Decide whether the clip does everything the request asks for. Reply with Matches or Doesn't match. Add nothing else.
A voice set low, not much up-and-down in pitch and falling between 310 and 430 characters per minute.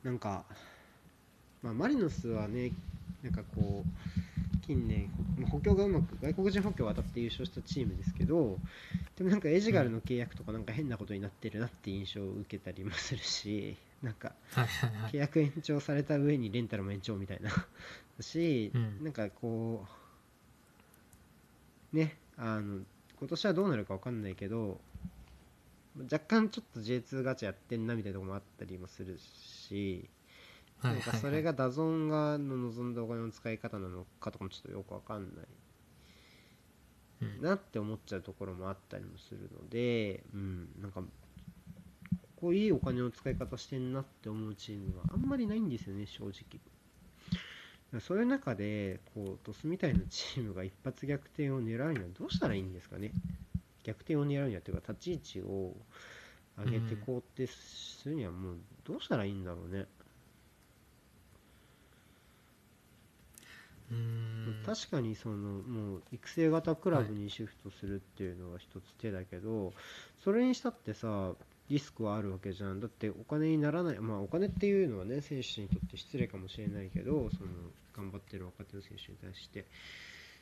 Doesn't match